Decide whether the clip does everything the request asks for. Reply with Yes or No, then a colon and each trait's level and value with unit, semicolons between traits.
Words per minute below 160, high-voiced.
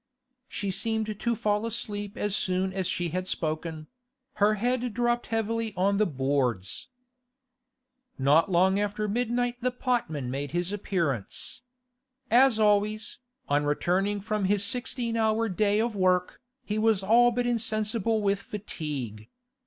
Yes: slow, 135 wpm; high, 205 Hz